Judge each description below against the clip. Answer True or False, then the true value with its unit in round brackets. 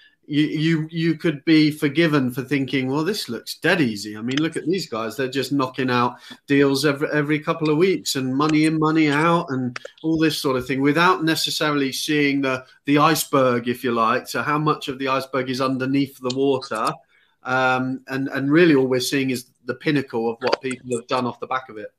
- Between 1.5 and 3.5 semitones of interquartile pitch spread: True (2.9 semitones)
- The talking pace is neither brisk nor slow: False (215 wpm)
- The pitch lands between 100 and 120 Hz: False (140 Hz)